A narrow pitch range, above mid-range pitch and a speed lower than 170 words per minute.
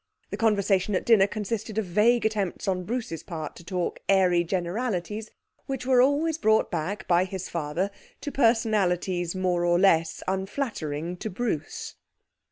No: average, 4.0 semitones; high, 195 Hz; average, 150 wpm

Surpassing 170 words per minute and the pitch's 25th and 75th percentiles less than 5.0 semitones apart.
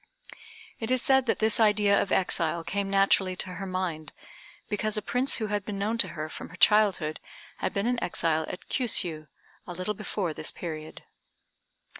Yes: average, 180 wpm; average, 3.9 semitones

